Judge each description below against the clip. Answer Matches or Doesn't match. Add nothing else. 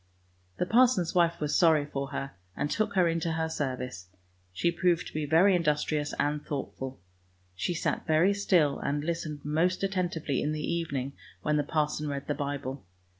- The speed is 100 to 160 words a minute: Doesn't match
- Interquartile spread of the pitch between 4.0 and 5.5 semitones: Doesn't match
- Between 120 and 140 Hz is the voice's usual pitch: Doesn't match